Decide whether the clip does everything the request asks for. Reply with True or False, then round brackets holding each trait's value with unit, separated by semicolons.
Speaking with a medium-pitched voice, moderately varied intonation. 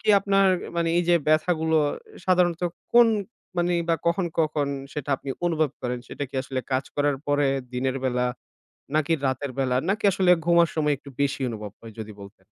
True (150 Hz; 4.6 semitones)